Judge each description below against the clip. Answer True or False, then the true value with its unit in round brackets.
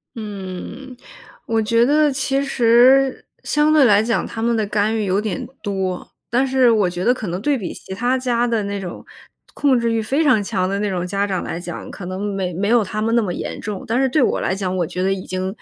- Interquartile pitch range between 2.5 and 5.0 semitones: True (4.3 semitones)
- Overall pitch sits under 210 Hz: False (215 Hz)